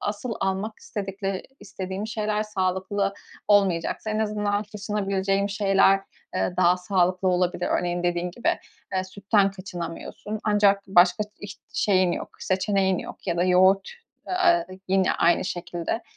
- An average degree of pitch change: No, narrow, 2.1 semitones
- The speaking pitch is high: Yes, high, 195 Hz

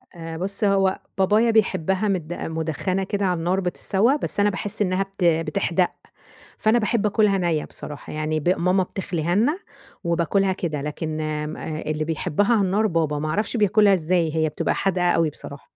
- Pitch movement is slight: No, average, 3.7 semitones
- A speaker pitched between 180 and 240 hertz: Yes, medium, 185 Hz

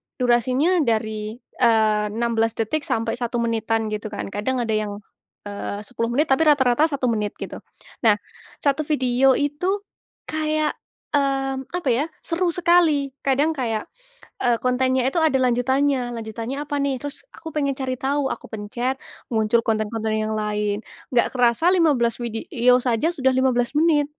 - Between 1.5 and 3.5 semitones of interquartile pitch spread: No, average, 4.1 semitones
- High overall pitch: Yes, very high, 250 Hz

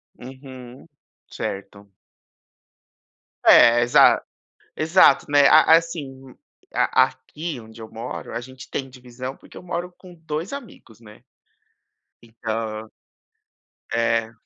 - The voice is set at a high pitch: No, low, 130 Hz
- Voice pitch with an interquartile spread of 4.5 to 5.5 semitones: Yes, average, 5.1 semitones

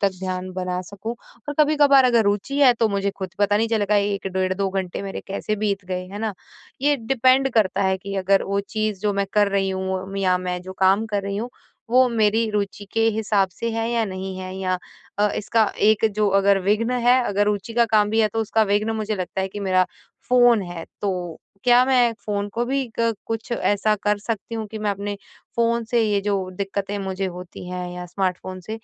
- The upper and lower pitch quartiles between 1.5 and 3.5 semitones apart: Yes, average, 2.8 semitones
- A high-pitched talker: Yes, high, 205 Hz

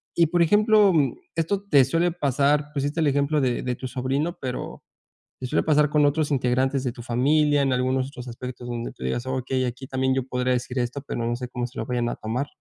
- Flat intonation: No, average, 3.0 semitones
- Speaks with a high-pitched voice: No, low, 130 Hz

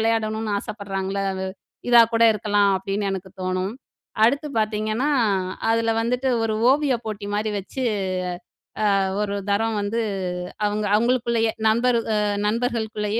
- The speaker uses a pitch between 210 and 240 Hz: Yes, high, 215 Hz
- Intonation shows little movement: Yes, narrow, 2.3 semitones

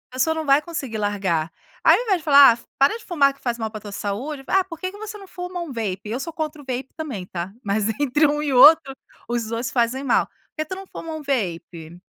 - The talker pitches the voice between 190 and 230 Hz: No, very high, 275 Hz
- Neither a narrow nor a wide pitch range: No, wide, 6.3 semitones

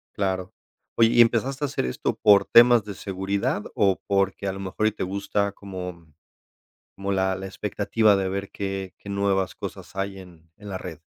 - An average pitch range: No, narrow, 1.4 semitones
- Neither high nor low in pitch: No, low, 100 Hz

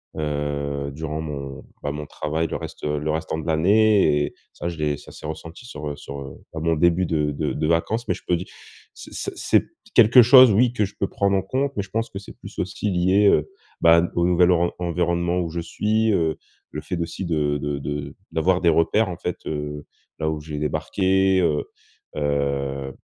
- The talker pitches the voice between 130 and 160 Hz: No, very low, 80 Hz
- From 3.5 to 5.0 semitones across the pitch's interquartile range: Yes, average, 4.0 semitones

